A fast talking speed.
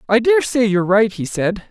Yes: fast, 210 wpm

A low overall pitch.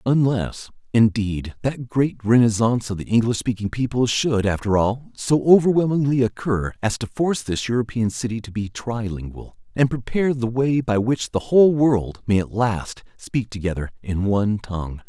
Yes: low, 115 Hz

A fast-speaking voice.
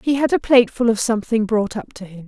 Yes: fast, 265 wpm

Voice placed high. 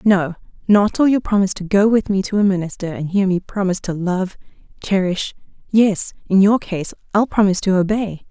Yes: high, 195 Hz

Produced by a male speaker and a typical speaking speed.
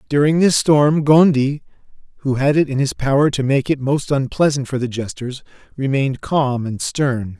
Yes: male; average, 180 wpm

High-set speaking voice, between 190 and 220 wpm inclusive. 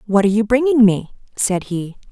Yes: high, 210 Hz; average, 200 wpm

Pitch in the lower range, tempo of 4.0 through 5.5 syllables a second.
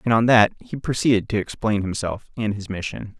Yes: low, 110 Hz; 5.4 syllables/s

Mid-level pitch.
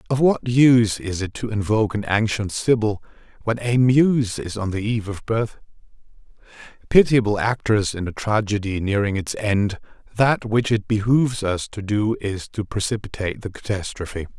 No: low, 110 Hz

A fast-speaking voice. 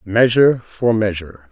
No: slow, 120 wpm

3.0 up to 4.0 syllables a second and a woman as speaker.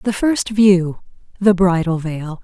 Yes: 3.6 syllables/s; female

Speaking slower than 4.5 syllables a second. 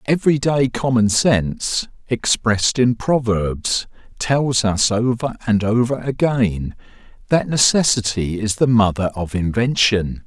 Yes: 4.0 syllables/s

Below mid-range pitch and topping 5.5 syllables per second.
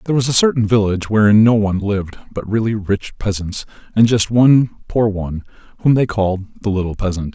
Yes: low, 105 Hz; 5.9 syllables/s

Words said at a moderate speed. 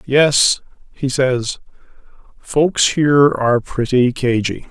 No: slow, 100 wpm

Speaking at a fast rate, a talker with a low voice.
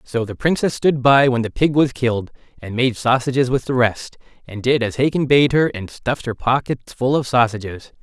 Yes: fast, 215 wpm; low, 125 Hz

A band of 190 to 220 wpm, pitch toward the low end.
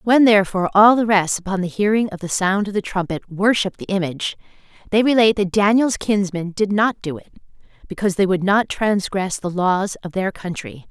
No: average, 200 wpm; high, 195 Hz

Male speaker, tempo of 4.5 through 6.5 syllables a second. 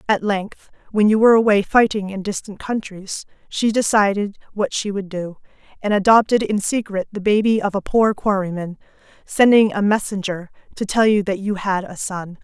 No: female; 5.0 syllables/s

